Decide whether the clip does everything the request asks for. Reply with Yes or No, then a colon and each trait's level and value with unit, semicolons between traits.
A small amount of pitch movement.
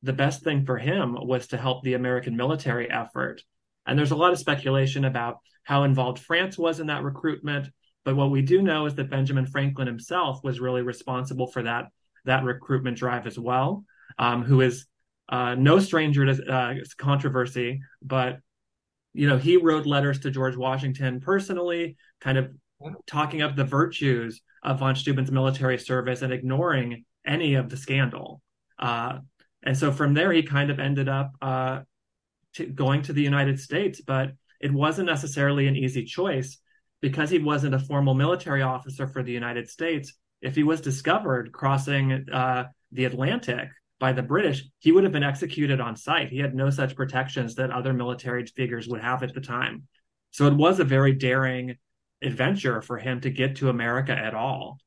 Yes: narrow, 2.0 semitones